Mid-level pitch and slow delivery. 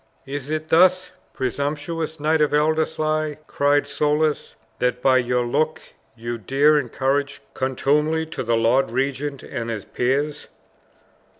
Yes: medium, 145 Hz; slow, 125 wpm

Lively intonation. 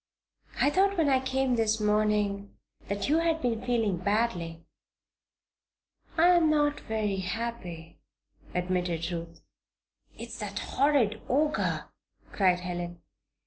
Yes: wide, 6.8 semitones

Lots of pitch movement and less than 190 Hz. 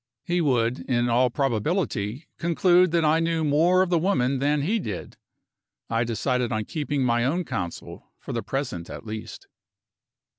Yes: wide, 5.9 semitones; low, 135 Hz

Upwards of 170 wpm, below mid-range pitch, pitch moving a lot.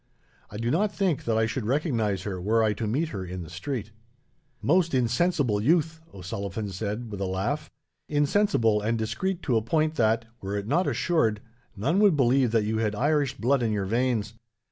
Yes: average, 190 wpm; low, 115 Hz; wide, 6.0 semitones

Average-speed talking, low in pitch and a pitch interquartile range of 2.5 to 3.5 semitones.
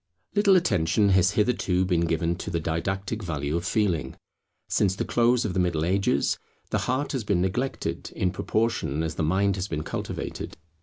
No: average, 175 wpm; very low, 95 Hz; average, 4.2 semitones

